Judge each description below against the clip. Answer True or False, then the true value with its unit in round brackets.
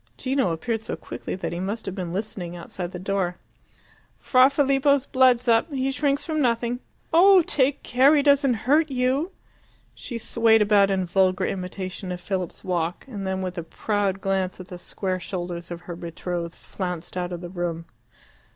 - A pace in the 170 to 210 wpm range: True (180 wpm)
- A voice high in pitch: True (195 Hz)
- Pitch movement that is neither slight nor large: False (6.3 semitones)